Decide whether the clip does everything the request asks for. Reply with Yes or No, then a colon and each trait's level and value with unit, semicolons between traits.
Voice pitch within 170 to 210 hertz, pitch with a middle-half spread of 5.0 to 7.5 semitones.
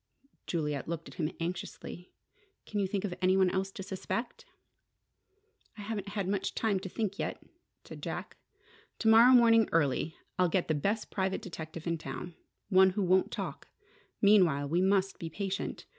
No: high, 190 Hz; average, 3.2 semitones